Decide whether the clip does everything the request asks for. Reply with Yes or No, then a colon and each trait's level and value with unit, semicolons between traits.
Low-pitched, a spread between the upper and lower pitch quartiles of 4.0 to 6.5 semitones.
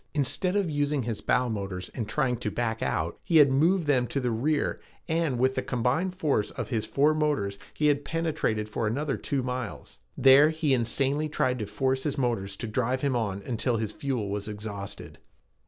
Yes: low, 130 Hz; average, 4.8 semitones